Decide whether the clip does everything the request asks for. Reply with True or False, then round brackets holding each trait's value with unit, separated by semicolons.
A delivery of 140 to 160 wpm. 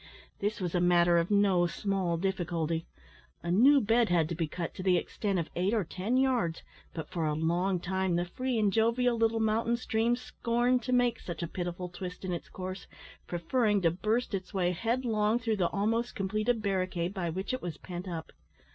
False (200 wpm)